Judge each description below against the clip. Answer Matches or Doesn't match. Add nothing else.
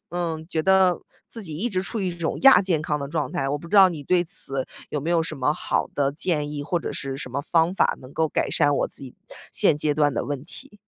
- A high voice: Doesn't match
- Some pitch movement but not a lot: Matches